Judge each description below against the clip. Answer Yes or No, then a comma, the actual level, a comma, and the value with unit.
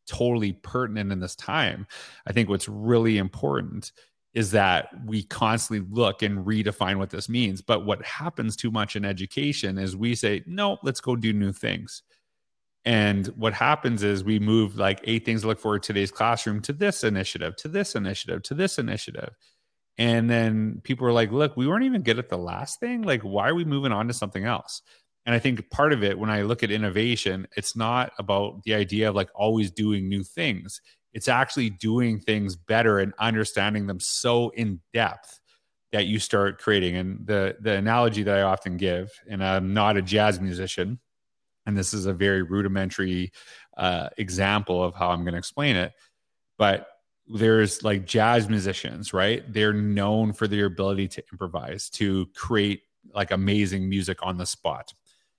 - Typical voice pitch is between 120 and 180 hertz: No, low, 105 Hz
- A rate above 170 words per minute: Yes, average, 185 wpm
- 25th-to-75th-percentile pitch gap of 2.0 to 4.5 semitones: Yes, average, 2.8 semitones